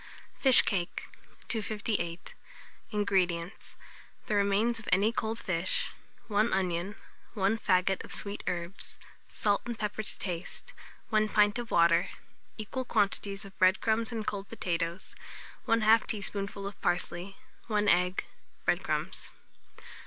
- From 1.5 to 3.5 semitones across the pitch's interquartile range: Yes, average, 2.9 semitones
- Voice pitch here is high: Yes, high, 200 Hz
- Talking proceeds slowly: Yes, slow, 125 wpm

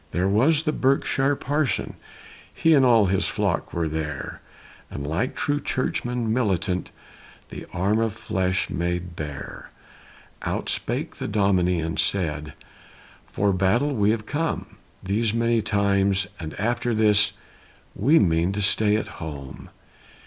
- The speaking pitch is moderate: No, low, 100 Hz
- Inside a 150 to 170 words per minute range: No, slow, 135 wpm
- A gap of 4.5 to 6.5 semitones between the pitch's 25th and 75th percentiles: Yes, average, 4.9 semitones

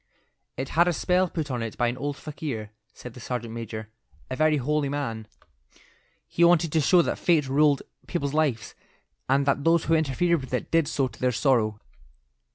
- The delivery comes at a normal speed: Yes, average, 190 wpm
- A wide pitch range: No, average, 4.2 semitones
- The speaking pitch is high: No, medium, 140 Hz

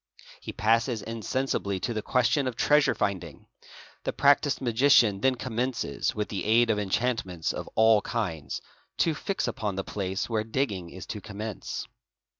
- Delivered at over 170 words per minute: No, average, 155 wpm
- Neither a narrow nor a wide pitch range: Yes, average, 4.2 semitones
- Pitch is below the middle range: Yes, low, 110 Hz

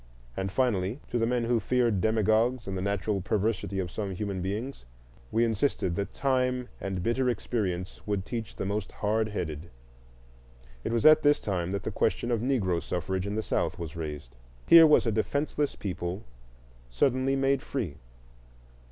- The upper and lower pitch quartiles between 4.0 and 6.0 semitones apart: Yes, average, 4.7 semitones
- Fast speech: No, average, 165 wpm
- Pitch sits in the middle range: No, low, 105 Hz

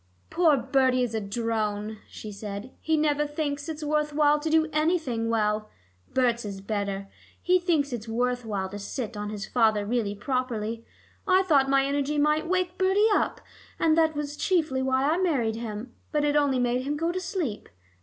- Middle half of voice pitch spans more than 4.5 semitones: Yes, wide, 5.6 semitones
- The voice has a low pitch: No, very high, 265 Hz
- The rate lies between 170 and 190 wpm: Yes, average, 185 wpm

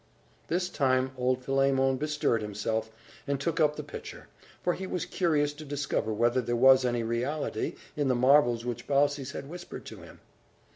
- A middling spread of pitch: Yes, average, 3.4 semitones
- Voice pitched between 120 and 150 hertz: Yes, low, 135 Hz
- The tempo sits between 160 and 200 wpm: Yes, average, 175 wpm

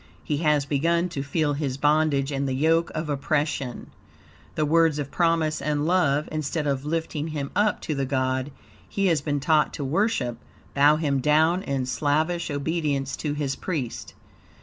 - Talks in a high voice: No, medium, 150 Hz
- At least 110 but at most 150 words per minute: No, average, 170 wpm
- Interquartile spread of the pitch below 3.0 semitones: Yes, narrow, 2.4 semitones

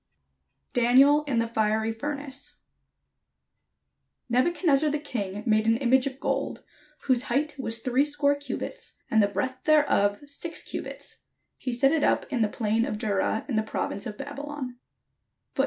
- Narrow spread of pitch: No, average, 4.4 semitones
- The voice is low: No, very high, 255 Hz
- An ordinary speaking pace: Yes, average, 150 wpm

